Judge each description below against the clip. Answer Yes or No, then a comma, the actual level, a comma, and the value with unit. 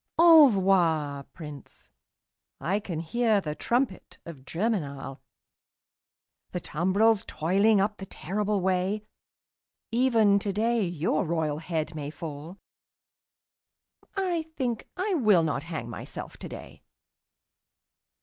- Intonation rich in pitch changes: Yes, wide, 5.7 semitones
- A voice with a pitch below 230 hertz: Yes, high, 190 Hz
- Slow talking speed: Yes, slow, 100 wpm